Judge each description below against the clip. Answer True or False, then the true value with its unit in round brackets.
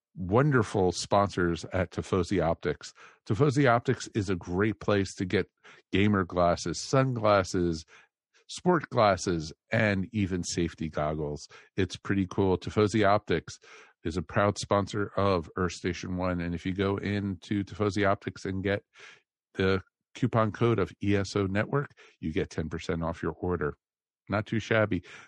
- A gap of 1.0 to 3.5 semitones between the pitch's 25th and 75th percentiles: True (2.8 semitones)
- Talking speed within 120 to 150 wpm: True (140 wpm)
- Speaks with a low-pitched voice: True (100 Hz)